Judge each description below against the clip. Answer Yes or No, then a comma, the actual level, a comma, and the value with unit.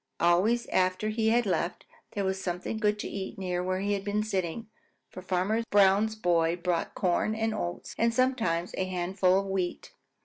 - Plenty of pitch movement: No, average, 3.1 semitones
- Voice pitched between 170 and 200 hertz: Yes, high, 190 Hz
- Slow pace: No, average, 180 wpm